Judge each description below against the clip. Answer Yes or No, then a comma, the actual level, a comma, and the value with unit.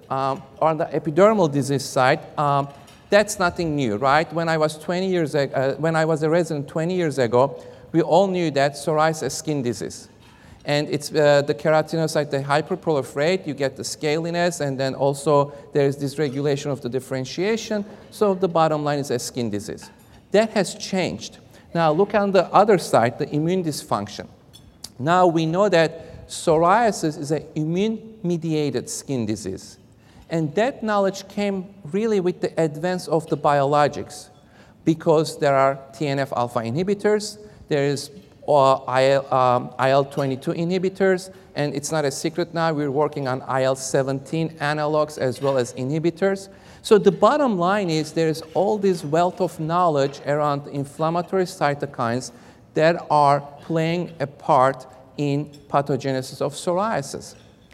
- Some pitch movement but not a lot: Yes, average, 4.1 semitones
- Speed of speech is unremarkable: Yes, average, 150 wpm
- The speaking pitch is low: No, medium, 155 Hz